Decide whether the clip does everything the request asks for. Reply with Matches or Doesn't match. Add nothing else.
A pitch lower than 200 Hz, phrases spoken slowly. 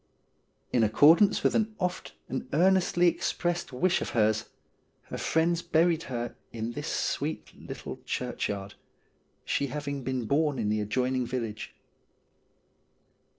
Matches